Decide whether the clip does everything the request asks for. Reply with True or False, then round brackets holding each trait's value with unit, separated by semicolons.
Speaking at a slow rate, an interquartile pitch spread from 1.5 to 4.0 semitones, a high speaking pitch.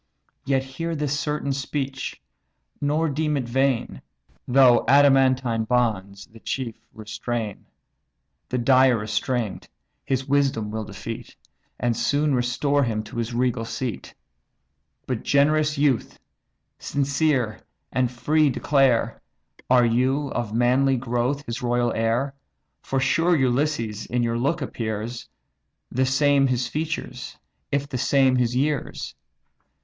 False (125 wpm; 3.1 semitones; 130 Hz)